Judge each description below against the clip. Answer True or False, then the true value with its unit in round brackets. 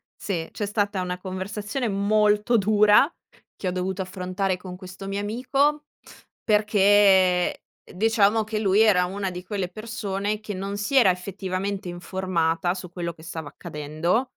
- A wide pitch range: False (2.5 semitones)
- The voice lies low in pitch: False (195 Hz)